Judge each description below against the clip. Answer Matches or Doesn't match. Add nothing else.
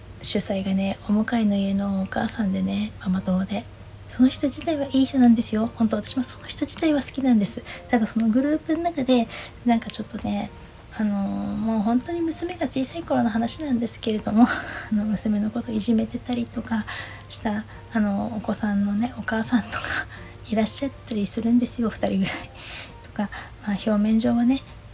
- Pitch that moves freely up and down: Doesn't match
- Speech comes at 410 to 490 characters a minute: Doesn't match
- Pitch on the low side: Doesn't match